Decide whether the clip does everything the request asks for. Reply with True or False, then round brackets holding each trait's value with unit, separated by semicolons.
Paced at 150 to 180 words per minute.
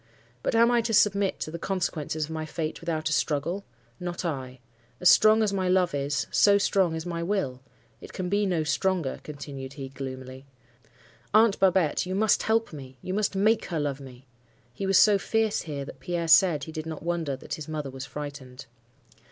False (195 wpm)